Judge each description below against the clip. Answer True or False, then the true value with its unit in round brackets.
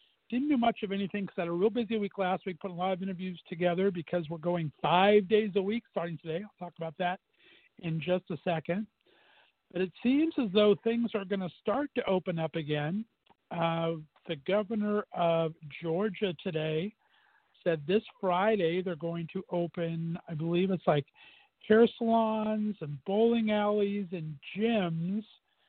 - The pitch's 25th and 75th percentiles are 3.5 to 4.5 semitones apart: True (4.1 semitones)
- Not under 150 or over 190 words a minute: True (175 wpm)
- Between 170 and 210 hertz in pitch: True (190 Hz)